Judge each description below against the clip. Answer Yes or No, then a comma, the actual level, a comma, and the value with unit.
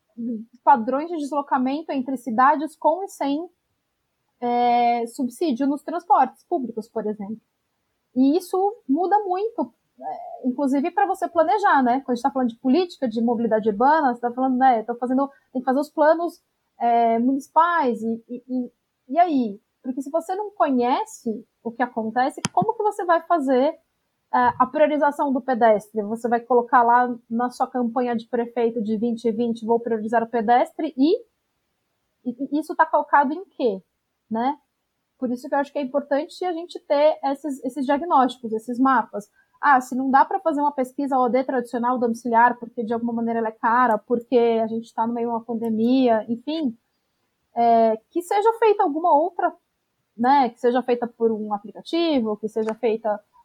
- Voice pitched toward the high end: Yes, very high, 260 Hz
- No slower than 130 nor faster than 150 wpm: No, average, 170 wpm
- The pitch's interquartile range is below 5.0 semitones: Yes, average, 4.6 semitones